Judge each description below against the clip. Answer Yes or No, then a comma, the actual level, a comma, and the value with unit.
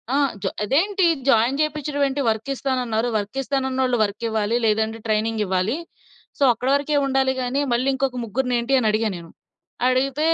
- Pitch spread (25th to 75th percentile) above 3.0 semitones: Yes, average, 3.7 semitones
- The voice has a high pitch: Yes, very high, 250 Hz